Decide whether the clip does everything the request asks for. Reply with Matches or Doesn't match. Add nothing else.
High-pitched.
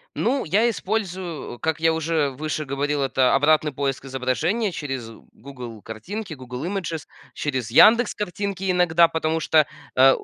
Doesn't match